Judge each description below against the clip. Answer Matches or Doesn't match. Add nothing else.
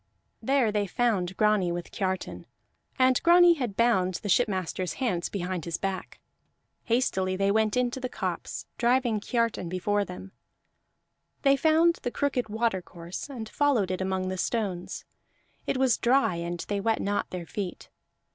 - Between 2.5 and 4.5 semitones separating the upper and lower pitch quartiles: Doesn't match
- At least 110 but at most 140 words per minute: Doesn't match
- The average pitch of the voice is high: Matches